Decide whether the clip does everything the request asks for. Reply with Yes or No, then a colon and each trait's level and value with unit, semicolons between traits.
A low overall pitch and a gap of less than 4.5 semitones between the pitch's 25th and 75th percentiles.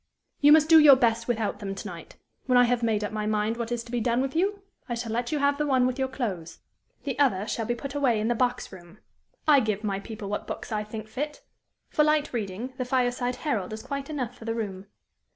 No: high, 240 Hz; average, 3.9 semitones